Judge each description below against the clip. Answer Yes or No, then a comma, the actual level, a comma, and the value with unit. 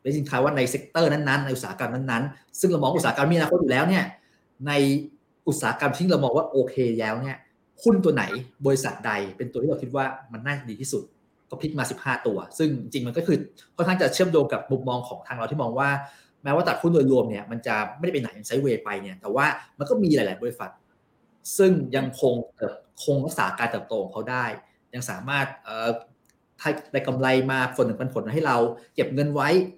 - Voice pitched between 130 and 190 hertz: Yes, low, 135 Hz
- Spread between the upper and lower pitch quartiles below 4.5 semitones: Yes, average, 3.4 semitones